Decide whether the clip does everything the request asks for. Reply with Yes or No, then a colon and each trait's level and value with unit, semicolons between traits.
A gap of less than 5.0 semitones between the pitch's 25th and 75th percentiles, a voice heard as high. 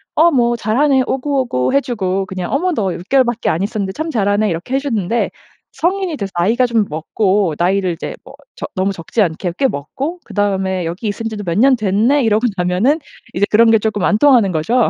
No: average, 5.3 semitones; high, 215 Hz